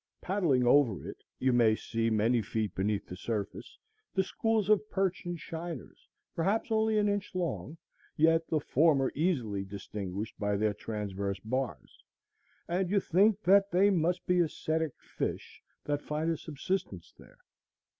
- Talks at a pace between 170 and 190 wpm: No, average, 150 wpm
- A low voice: No, medium, 155 Hz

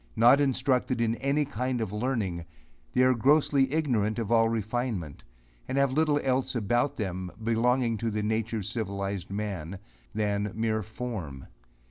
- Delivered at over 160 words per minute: No, average, 150 wpm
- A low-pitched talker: Yes, low, 115 Hz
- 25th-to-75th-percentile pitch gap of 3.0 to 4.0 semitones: Yes, average, 3.7 semitones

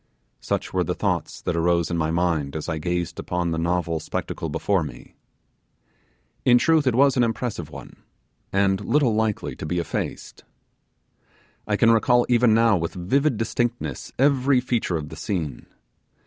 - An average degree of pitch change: No, wide, 6.4 semitones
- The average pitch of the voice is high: No, very low, 95 Hz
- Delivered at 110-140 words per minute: No, average, 160 wpm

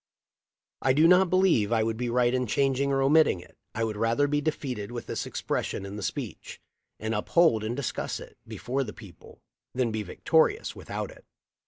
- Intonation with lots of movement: No, average, 4.6 semitones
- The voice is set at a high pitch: No, low, 125 Hz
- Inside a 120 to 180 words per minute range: No, average, 190 wpm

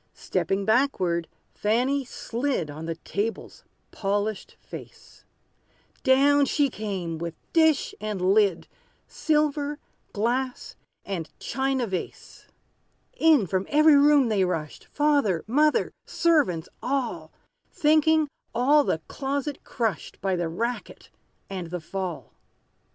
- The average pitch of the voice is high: Yes, high, 230 Hz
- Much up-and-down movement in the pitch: Yes, wide, 7.4 semitones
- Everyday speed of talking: No, slow, 110 wpm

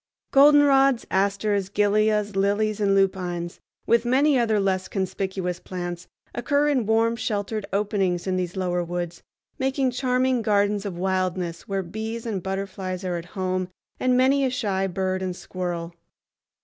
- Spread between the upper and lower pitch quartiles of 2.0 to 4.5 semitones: Yes, average, 3.7 semitones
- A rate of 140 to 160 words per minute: Yes, average, 145 wpm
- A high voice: Yes, high, 195 Hz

